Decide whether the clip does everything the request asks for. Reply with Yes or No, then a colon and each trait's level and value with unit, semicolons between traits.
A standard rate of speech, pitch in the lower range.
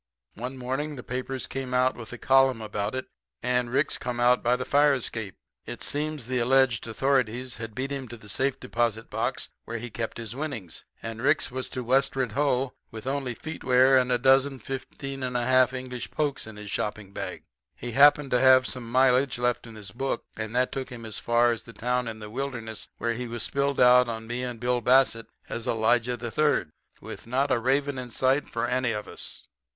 No: fast, 210 wpm; low, 125 Hz